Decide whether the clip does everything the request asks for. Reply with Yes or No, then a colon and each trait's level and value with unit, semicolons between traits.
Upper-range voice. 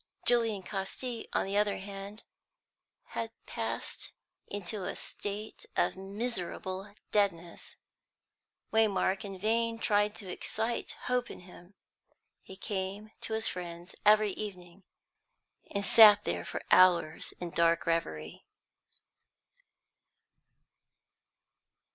Yes: high, 200 Hz